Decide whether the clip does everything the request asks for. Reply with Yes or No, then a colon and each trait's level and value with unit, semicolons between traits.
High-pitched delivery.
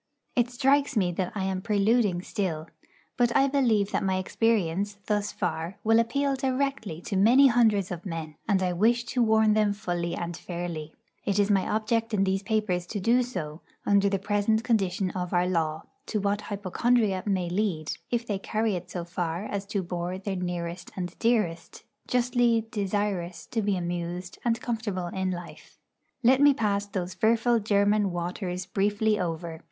Yes: high, 200 Hz